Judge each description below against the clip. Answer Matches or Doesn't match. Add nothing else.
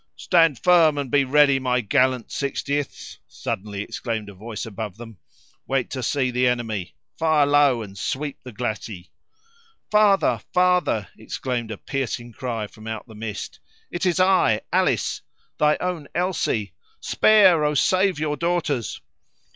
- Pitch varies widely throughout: Matches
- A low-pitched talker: Matches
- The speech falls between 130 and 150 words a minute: Matches